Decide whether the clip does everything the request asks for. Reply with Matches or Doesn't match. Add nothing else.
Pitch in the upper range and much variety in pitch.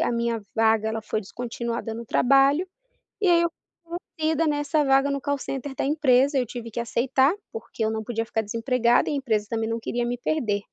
Doesn't match